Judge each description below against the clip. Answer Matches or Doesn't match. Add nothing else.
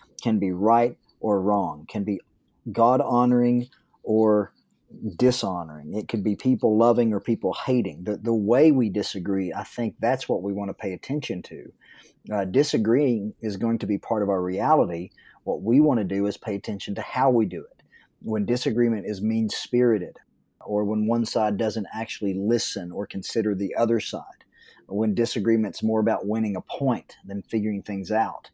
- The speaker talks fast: Doesn't match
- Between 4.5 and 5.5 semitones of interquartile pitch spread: Doesn't match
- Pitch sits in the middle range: Doesn't match